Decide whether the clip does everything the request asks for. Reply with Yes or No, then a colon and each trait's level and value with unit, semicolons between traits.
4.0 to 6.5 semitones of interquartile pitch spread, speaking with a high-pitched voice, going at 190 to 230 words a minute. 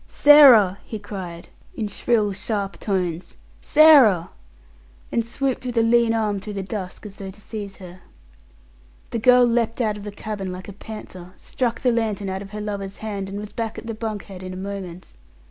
No: average, 2.9 semitones; high, 210 Hz; average, 195 wpm